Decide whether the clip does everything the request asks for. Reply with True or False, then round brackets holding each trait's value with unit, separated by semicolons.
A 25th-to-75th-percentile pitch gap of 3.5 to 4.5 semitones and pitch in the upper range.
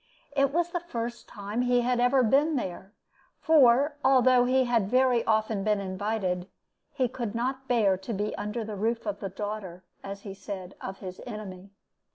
True (4.1 semitones; 225 Hz)